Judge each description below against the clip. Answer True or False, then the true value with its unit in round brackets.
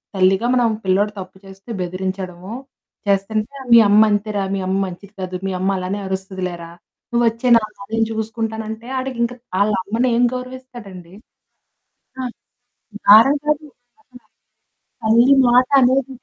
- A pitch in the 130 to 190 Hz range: False (215 Hz)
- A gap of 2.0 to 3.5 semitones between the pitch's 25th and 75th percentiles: False (3.9 semitones)